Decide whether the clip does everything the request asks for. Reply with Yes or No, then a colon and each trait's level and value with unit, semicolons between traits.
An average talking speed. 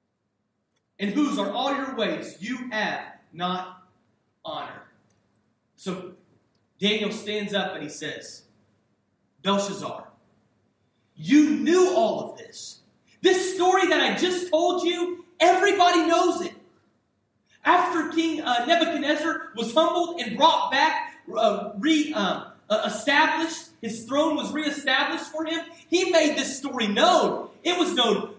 No: slow, 130 wpm